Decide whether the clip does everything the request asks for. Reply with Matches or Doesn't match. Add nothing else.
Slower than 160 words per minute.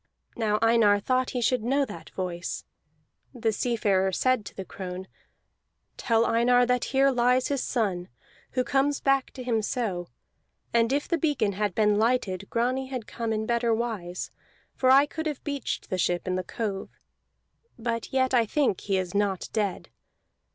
Doesn't match